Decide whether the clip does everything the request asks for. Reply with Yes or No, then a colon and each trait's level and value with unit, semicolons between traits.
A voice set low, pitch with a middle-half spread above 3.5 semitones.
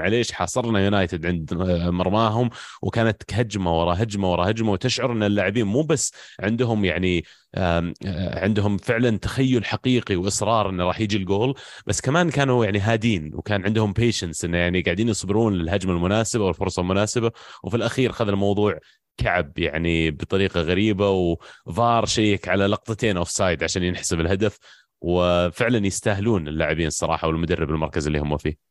Yes: low, 100 Hz; average, 4.1 semitones